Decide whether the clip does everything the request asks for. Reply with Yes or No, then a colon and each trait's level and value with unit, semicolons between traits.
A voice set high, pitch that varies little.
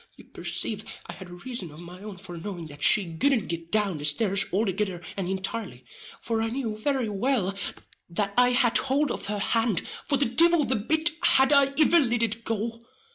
No: high, 215 Hz; average, 5.2 semitones